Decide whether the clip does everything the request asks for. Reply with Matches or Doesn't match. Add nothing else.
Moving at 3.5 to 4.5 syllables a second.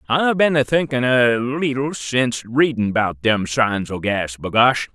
Matches